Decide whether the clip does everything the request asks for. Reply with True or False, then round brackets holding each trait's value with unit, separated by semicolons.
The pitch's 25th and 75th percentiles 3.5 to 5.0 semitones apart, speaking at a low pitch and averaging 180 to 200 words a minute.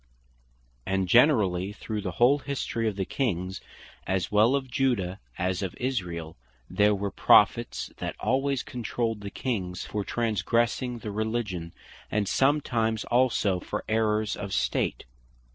False (4.3 semitones; 105 Hz; 145 wpm)